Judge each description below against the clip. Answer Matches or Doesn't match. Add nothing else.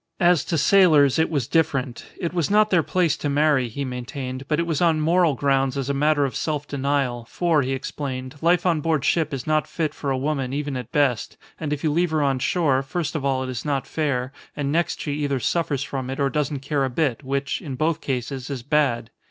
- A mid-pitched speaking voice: Matches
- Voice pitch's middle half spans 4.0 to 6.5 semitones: Doesn't match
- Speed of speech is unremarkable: Doesn't match